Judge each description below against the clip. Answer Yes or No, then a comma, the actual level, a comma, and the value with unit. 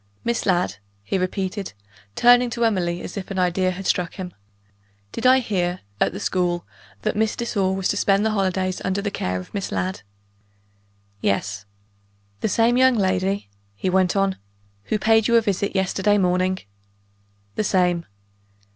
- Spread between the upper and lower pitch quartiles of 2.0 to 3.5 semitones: Yes, narrow, 2.5 semitones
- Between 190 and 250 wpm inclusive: No, average, 165 wpm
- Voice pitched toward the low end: No, high, 190 Hz